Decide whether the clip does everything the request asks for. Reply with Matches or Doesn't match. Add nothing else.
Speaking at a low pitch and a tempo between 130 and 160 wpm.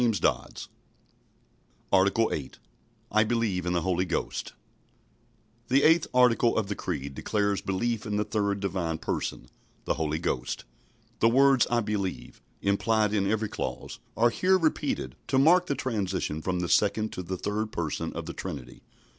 Matches